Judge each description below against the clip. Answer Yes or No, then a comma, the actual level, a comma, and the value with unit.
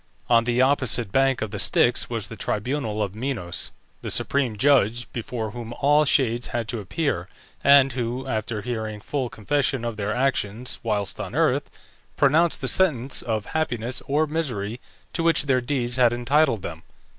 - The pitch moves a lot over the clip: No, average, 3.9 semitones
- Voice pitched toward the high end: No, low, 120 Hz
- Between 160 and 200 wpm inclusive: Yes, average, 170 wpm